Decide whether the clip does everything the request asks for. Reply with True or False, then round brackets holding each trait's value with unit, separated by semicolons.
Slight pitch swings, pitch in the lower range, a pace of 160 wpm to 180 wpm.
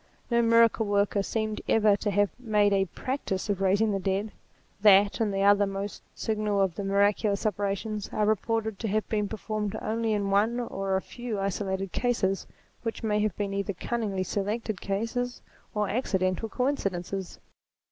False (2.1 semitones; 205 Hz; 165 wpm)